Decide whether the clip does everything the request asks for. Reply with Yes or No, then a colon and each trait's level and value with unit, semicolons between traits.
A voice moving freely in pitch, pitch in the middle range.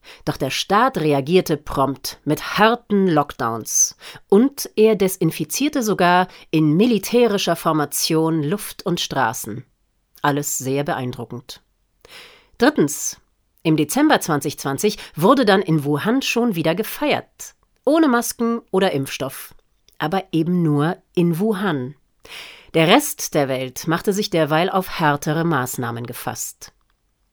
Yes: wide, 6.4 semitones; medium, 170 Hz